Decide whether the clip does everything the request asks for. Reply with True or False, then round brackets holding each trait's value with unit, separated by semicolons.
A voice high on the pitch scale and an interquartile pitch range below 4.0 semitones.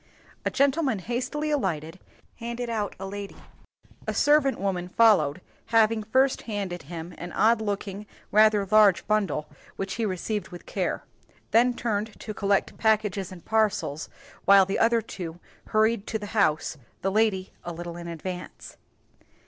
True (205 Hz; 3.6 semitones)